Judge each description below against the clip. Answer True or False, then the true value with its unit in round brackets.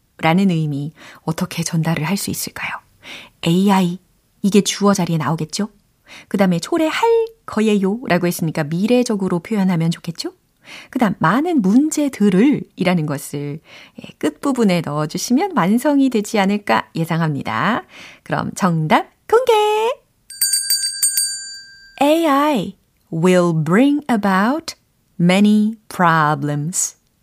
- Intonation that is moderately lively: False (8.7 semitones)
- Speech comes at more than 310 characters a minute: False (280 characters per minute)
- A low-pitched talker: False (200 Hz)